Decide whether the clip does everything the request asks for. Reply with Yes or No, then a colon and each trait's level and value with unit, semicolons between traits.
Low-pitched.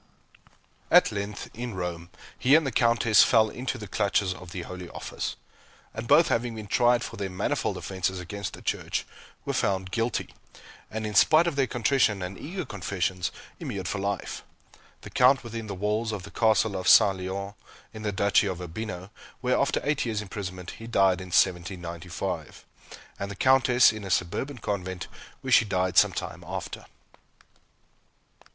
Yes: low, 100 Hz